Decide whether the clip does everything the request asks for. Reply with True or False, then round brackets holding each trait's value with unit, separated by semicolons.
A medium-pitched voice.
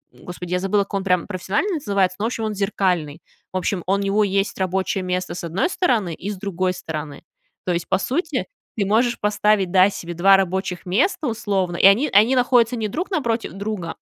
False (195 Hz)